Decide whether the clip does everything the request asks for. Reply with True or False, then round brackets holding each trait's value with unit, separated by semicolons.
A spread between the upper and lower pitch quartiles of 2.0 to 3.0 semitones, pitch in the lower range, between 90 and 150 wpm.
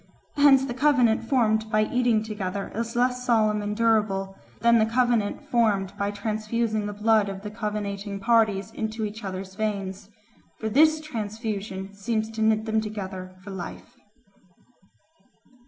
False (2.4 semitones; 215 Hz; 145 wpm)